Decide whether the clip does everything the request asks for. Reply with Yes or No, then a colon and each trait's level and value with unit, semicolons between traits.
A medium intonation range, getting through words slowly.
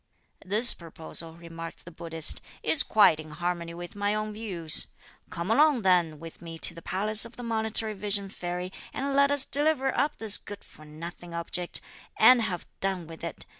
No: average, 4.7 semitones; average, 180 wpm